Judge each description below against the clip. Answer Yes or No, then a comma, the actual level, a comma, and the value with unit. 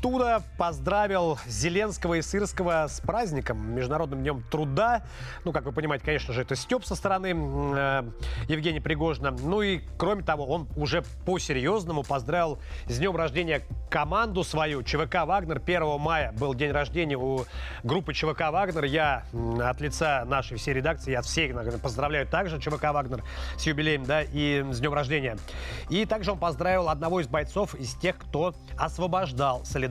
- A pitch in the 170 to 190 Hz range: No, medium, 155 Hz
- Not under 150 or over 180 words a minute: Yes, average, 155 wpm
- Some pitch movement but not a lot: Yes, average, 4.3 semitones